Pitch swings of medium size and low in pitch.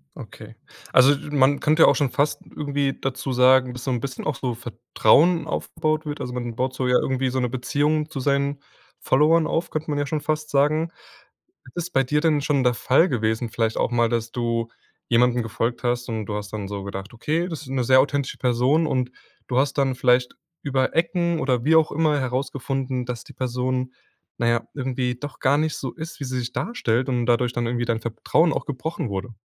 Yes: average, 3.3 semitones; low, 130 Hz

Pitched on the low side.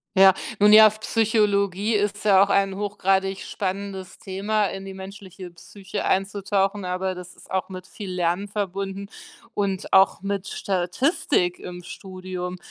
No: high, 195 Hz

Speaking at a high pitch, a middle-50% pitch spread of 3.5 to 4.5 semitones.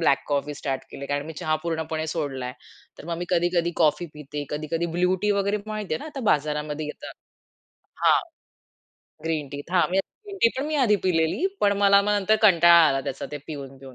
No: medium, 160 Hz; average, 4.1 semitones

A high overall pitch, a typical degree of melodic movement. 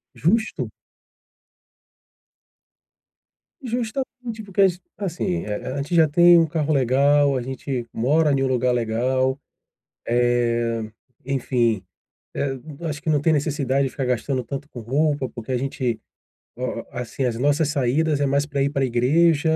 No: medium, 140 Hz; average, 3.7 semitones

